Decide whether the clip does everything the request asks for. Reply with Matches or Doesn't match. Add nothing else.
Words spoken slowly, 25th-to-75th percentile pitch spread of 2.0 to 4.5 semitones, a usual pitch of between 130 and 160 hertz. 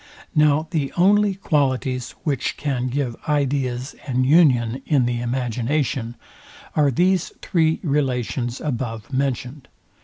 Matches